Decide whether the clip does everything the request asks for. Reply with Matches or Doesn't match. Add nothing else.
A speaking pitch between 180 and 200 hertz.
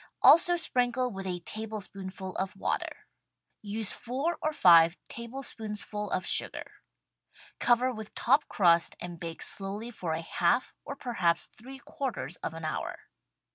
Doesn't match